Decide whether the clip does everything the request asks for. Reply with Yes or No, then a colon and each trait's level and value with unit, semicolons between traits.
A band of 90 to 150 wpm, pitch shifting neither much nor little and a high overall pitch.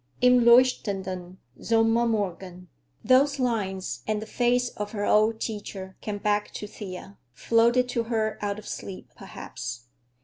Yes: slow, 135 wpm; average, 3.4 semitones; high, 215 Hz